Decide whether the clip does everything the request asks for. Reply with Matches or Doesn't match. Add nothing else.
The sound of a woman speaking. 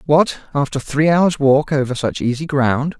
Doesn't match